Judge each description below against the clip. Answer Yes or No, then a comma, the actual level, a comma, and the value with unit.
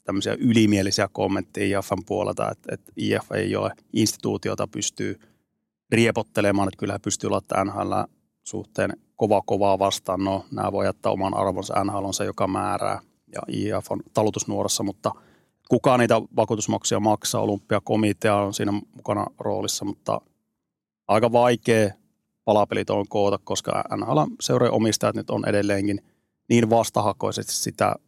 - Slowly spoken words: No, average, 135 wpm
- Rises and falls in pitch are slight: Yes, narrow, 2.0 semitones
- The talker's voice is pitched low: Yes, low, 105 Hz